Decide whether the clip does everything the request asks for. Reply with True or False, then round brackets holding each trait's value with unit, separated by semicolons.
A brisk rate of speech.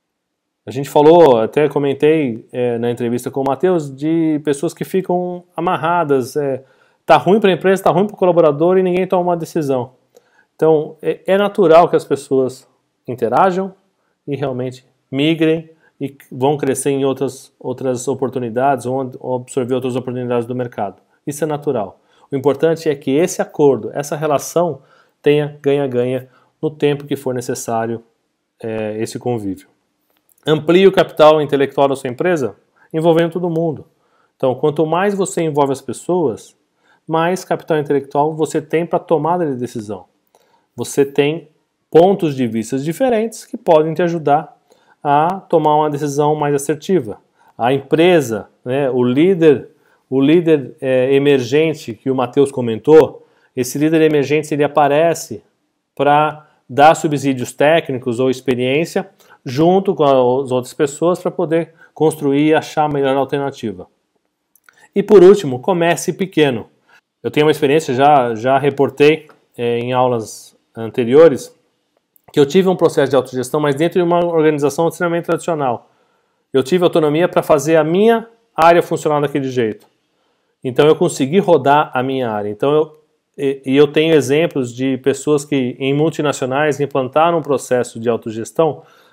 False (150 wpm)